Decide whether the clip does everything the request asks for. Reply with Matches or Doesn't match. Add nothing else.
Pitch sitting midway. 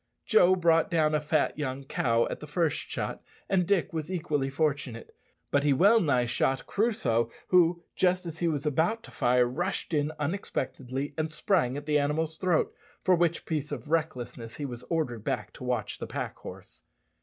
Matches